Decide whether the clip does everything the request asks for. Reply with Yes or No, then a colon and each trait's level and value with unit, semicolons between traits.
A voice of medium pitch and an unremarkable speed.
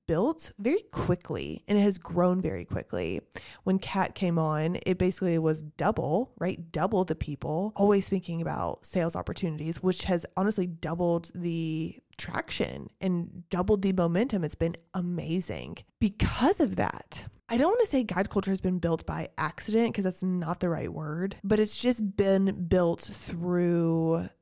Yes: medium, 180 Hz; average, 160 wpm